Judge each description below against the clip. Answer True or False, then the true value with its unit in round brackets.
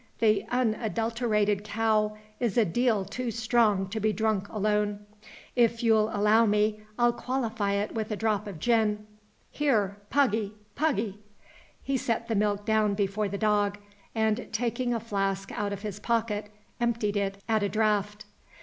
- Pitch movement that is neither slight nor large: False (1.9 semitones)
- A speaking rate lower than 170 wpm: True (155 wpm)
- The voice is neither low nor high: False (215 Hz)